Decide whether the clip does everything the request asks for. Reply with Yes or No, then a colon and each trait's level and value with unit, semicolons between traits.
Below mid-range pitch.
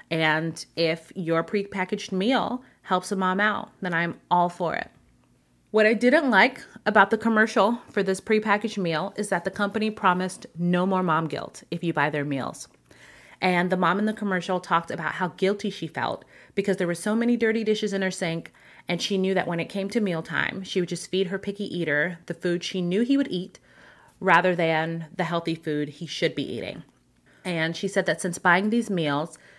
No: medium, 185 Hz